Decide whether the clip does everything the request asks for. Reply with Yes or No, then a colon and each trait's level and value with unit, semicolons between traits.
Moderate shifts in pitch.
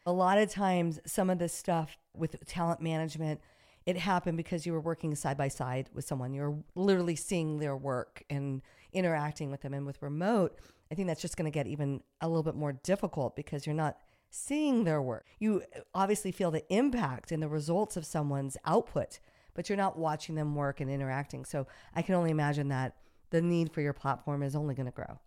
Yes: average, 3.6 semitones